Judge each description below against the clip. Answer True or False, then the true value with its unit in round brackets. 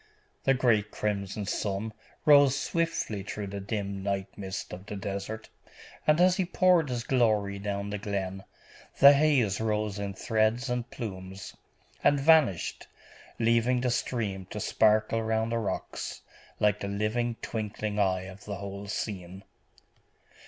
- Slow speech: False (145 wpm)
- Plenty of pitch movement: False (3.4 semitones)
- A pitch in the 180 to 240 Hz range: False (105 Hz)